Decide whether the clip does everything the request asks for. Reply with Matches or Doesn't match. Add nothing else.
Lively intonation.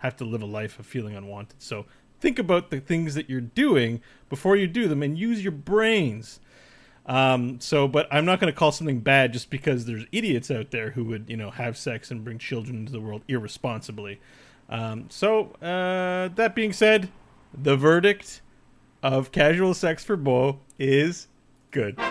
Matches